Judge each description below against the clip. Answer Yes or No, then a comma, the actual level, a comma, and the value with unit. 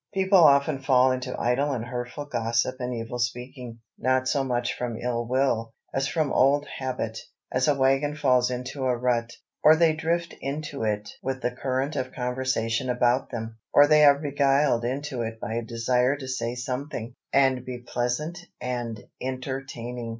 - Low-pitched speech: Yes, low, 130 Hz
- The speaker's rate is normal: Yes, average, 170 wpm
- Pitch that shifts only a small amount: Yes, narrow, 2.3 semitones